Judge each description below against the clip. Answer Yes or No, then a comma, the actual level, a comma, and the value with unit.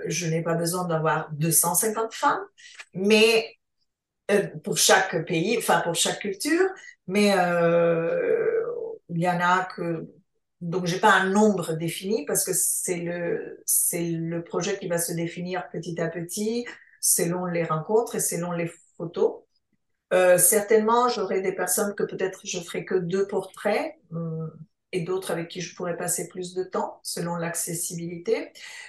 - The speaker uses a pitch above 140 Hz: Yes, medium, 185 Hz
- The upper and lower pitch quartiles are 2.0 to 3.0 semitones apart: No, average, 4.2 semitones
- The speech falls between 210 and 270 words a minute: No, average, 155 wpm